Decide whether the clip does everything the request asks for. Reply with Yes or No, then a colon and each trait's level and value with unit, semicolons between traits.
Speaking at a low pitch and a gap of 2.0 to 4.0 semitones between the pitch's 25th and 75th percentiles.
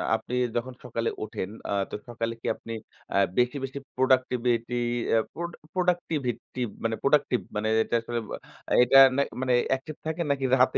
Yes: low, 125 Hz; average, 2.9 semitones